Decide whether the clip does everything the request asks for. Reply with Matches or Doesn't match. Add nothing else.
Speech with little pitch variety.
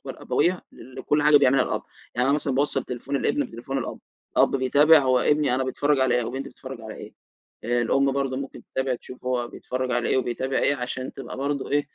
Matches